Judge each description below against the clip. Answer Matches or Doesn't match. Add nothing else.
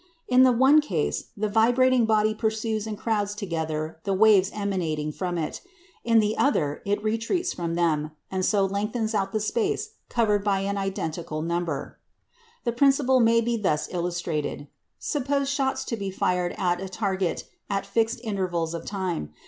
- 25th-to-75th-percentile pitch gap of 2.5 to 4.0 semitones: Doesn't match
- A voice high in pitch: Matches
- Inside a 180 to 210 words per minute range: Doesn't match